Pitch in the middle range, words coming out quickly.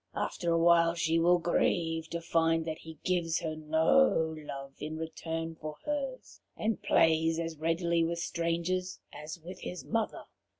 No: medium, 165 Hz; average, 160 wpm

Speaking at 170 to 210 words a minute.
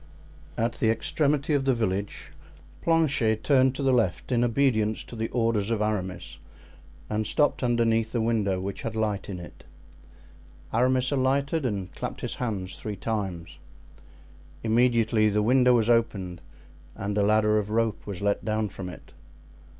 No: average, 155 wpm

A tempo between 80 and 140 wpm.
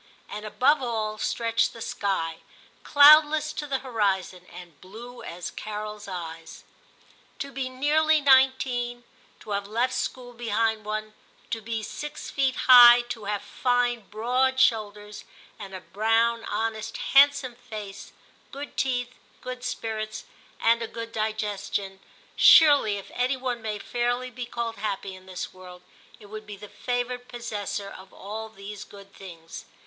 No: average, 150 wpm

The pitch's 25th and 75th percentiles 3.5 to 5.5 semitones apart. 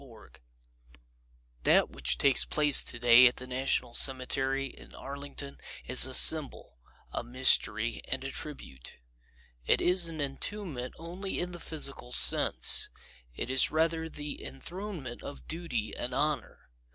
Yes: average, 4.2 semitones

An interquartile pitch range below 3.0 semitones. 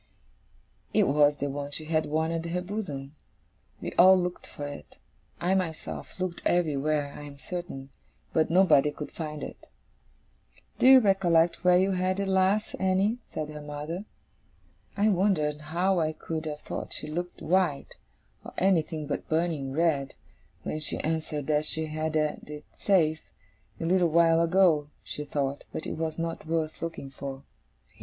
No: average, 3.3 semitones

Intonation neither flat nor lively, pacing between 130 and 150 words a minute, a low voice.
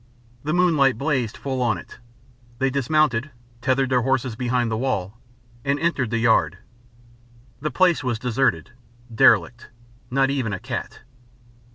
Yes: average, 3.3 semitones; average, 140 wpm; low, 130 Hz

